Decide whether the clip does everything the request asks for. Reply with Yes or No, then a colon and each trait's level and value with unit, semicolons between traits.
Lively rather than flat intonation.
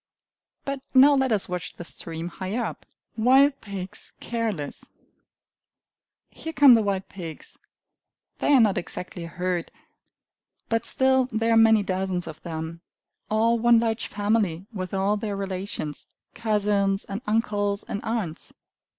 No: average, 3.8 semitones